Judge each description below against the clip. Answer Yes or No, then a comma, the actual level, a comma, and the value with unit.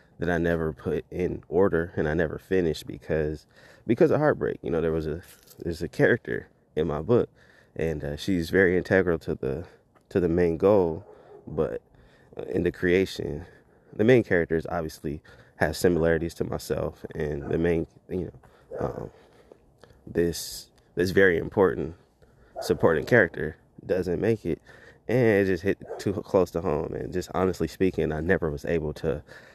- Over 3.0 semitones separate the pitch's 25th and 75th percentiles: No, narrow, 2.4 semitones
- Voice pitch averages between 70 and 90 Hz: Yes, very low, 85 Hz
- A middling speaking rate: Yes, average, 160 wpm